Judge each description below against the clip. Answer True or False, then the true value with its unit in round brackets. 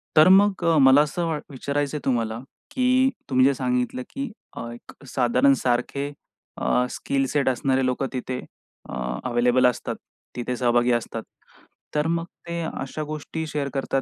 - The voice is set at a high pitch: False (135 Hz)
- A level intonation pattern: False (3.4 semitones)